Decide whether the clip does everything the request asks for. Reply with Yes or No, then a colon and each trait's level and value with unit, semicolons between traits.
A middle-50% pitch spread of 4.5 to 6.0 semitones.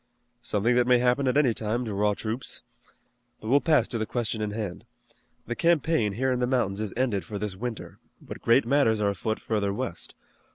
No: average, 3.1 semitones